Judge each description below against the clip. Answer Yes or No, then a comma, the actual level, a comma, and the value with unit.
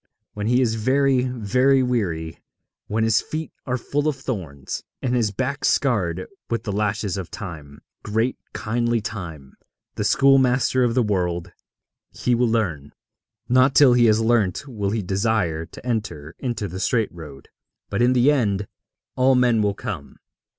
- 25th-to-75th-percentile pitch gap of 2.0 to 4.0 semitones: No, average, 4.7 semitones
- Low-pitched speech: Yes, low, 110 Hz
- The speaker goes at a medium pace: Yes, average, 160 wpm